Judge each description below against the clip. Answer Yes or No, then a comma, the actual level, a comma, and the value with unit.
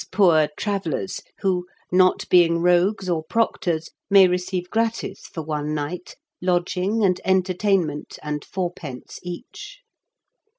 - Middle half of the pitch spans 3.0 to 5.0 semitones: No, narrow, 2.6 semitones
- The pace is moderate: No, slow, 125 wpm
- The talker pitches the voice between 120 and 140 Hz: No, medium, 180 Hz